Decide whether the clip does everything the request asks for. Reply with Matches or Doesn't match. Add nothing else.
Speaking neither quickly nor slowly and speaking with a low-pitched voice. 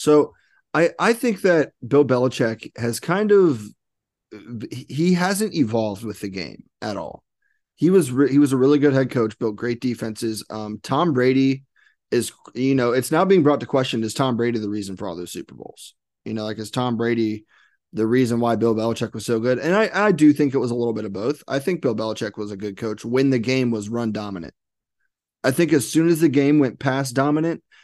Doesn't match